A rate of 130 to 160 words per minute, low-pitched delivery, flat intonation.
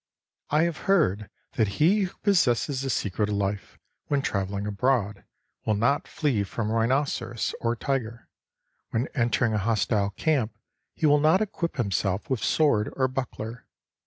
No: average, 150 wpm; low, 120 Hz; wide, 5.5 semitones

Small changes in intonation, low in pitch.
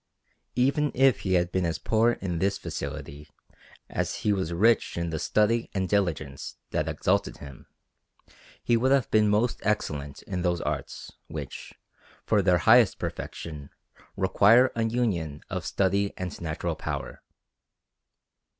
No: average, 5.2 semitones; very low, 95 Hz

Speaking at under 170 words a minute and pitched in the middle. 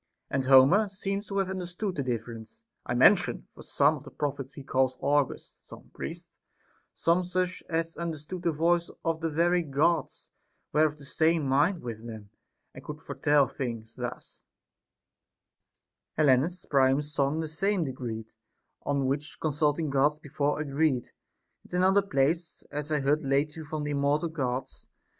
Yes: average, 155 wpm; medium, 150 Hz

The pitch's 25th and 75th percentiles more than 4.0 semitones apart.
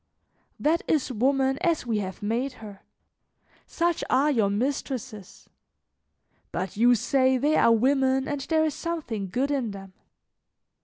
Yes: average, 4.6 semitones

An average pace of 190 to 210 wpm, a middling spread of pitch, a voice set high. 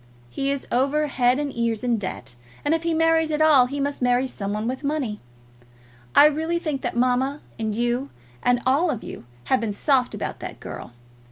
Yes: average, 200 wpm; average, 3.7 semitones; very high, 265 Hz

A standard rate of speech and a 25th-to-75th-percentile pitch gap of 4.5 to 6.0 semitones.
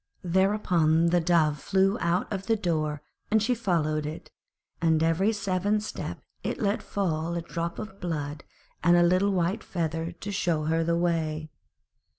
No: average, 160 wpm; average, 3.2 semitones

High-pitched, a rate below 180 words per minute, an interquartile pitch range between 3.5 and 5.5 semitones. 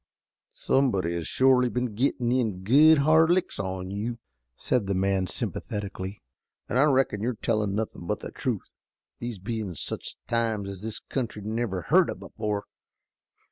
No: low, 110 Hz; average, 155 wpm; average, 4.3 semitones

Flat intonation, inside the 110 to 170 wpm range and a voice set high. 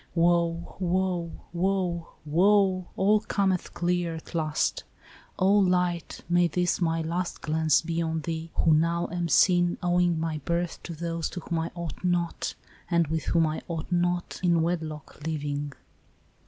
No: narrow, 1.6 semitones; average, 155 wpm; medium, 170 Hz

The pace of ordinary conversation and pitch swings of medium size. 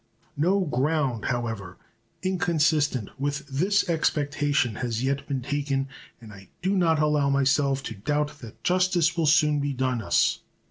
Yes: average, 145 wpm; average, 3.4 semitones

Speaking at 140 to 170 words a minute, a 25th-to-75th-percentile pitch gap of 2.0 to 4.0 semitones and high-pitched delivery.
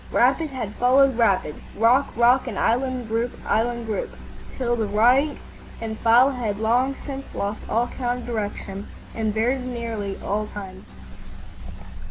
Yes: average, 145 wpm; average, 2.7 semitones; high, 235 Hz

